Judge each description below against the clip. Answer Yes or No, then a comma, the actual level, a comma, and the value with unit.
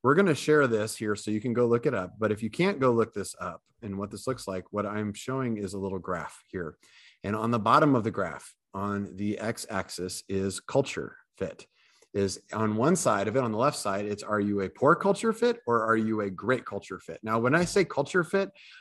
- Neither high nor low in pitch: No, low, 110 Hz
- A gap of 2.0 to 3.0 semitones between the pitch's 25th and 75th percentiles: No, average, 4.7 semitones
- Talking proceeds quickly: Yes, fast, 250 wpm